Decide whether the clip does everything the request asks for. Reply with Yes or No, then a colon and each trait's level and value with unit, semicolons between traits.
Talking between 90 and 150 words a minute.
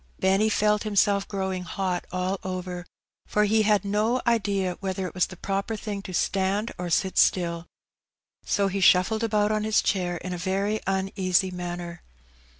No: average, 165 wpm